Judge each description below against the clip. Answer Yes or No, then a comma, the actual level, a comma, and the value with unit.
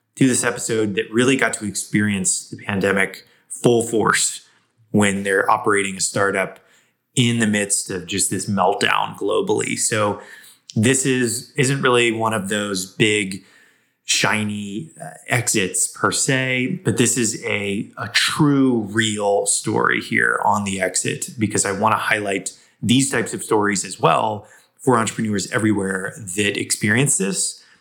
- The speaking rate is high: No, average, 145 wpm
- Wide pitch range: No, average, 3.7 semitones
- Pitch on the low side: Yes, low, 110 Hz